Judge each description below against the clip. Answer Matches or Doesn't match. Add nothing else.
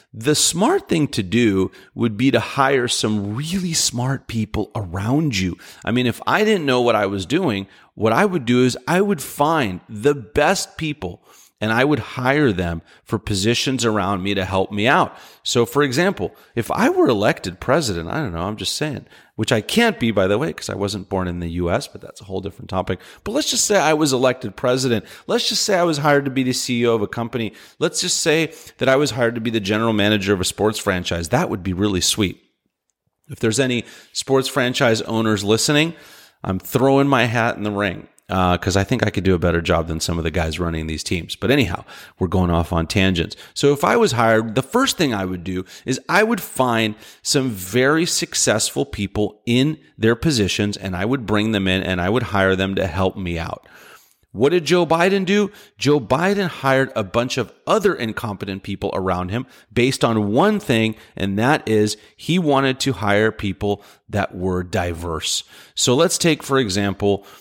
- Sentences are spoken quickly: Matches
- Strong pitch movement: Matches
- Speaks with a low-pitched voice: Matches